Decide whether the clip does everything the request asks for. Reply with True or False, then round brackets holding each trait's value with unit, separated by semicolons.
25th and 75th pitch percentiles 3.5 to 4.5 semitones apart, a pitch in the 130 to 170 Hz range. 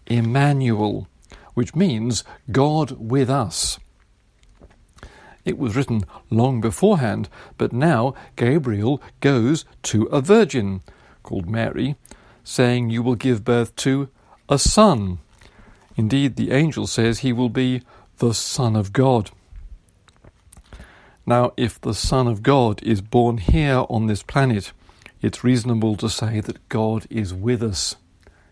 False (4.1 semitones; 115 Hz)